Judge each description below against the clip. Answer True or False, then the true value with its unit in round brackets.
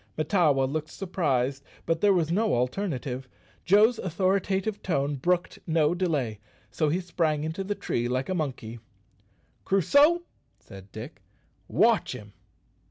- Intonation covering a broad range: True (6.0 semitones)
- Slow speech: True (130 wpm)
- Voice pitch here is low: False (160 Hz)